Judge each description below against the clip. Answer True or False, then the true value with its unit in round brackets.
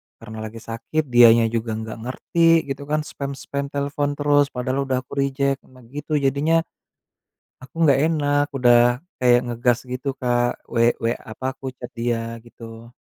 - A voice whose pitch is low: True (130 Hz)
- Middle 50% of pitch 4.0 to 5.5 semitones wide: False (3.1 semitones)